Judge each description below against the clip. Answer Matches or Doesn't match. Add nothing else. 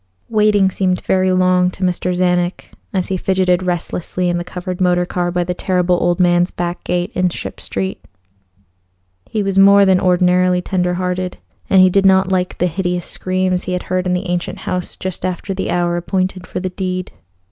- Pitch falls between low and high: Matches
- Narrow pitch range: Matches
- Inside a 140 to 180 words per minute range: Doesn't match